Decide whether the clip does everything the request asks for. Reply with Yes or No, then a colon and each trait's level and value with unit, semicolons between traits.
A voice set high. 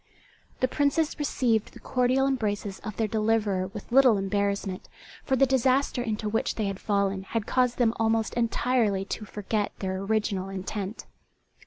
Yes: high, 220 Hz